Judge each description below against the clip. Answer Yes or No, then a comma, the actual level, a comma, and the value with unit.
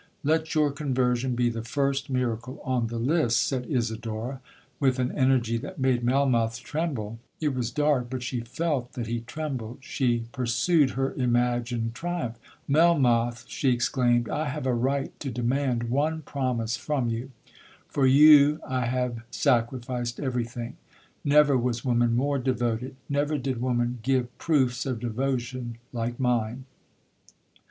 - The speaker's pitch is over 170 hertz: No, low, 125 Hz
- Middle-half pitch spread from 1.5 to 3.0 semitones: Yes, narrow, 2.6 semitones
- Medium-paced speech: No, slow, 130 wpm